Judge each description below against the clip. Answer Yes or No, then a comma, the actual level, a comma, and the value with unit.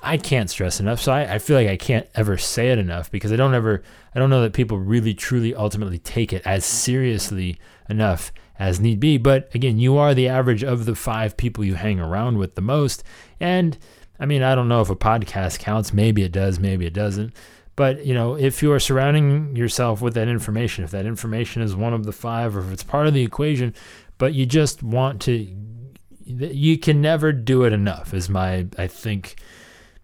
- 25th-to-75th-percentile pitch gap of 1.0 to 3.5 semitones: No, average, 4.7 semitones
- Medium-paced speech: No, fast, 215 wpm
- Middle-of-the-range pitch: No, low, 115 Hz